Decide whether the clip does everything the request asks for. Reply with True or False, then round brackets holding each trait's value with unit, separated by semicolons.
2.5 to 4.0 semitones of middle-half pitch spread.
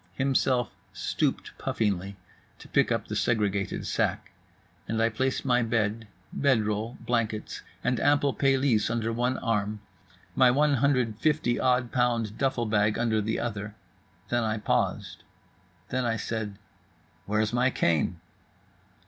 True (3.0 semitones)